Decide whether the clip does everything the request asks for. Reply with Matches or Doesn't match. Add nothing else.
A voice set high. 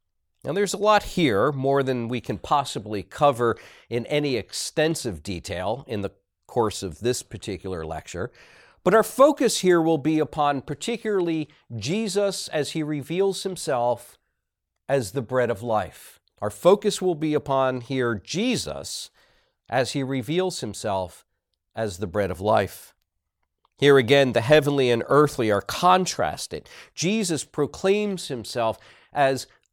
Doesn't match